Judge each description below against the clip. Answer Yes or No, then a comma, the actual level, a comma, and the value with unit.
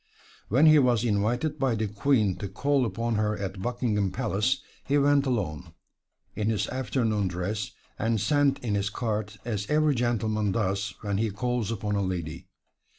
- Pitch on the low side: Yes, low, 110 Hz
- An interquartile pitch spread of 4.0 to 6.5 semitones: No, average, 3.6 semitones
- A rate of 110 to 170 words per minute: Yes, average, 165 wpm